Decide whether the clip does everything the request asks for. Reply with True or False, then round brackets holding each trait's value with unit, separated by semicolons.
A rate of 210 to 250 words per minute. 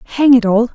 True (240 wpm)